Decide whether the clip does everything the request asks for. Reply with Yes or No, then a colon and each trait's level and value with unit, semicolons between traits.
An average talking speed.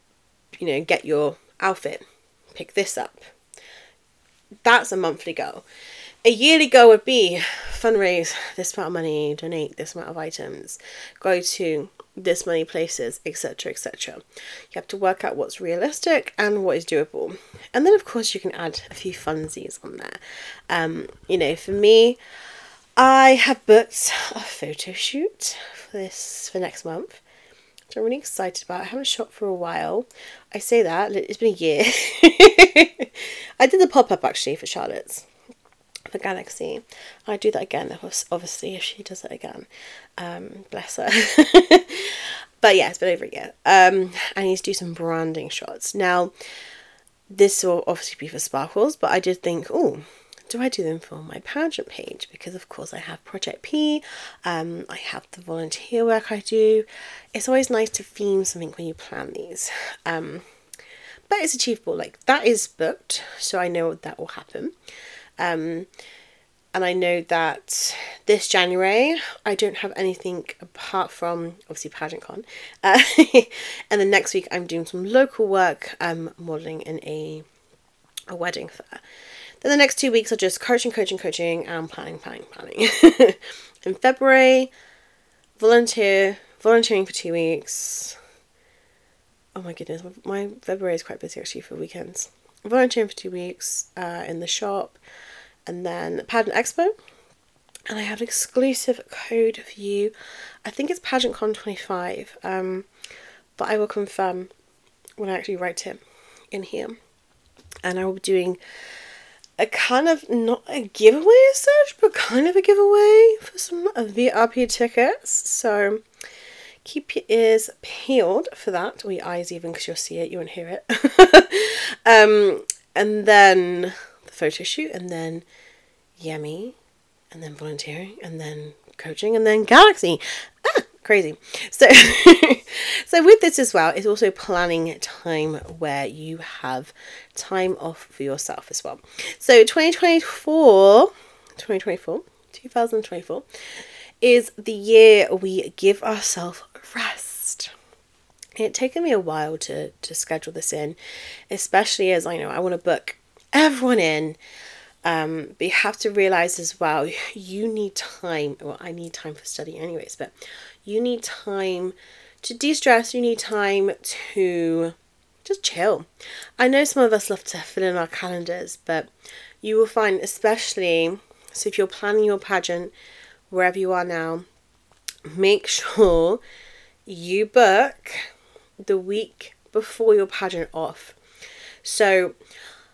Yes: average, 155 wpm